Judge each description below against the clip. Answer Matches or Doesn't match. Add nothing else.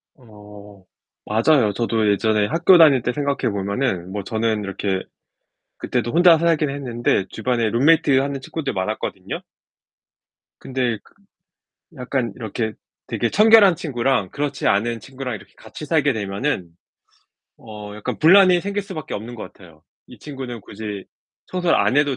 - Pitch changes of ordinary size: Doesn't match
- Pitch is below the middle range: Matches